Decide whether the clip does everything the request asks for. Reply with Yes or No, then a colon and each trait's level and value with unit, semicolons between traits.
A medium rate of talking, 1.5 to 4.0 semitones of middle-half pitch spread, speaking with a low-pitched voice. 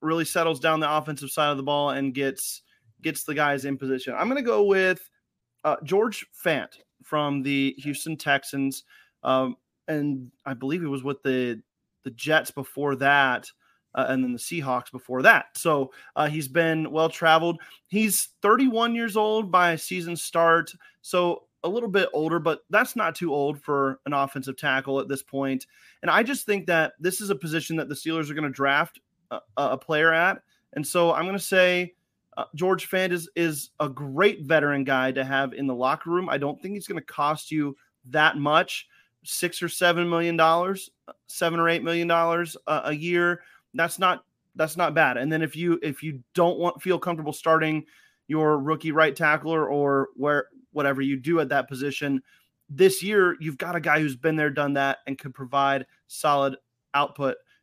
No: average, 190 wpm; average, 3.7 semitones; medium, 155 Hz